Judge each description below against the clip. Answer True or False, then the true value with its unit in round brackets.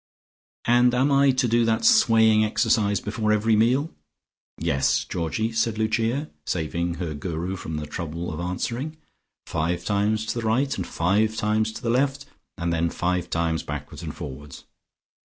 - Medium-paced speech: True (160 wpm)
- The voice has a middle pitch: False (110 Hz)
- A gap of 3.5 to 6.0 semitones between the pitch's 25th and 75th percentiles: True (5.4 semitones)